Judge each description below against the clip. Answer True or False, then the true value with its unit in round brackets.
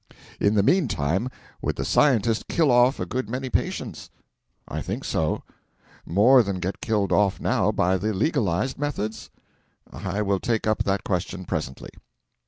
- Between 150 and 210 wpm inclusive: True (155 wpm)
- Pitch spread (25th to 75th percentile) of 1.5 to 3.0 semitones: False (4.5 semitones)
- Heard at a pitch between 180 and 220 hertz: False (105 Hz)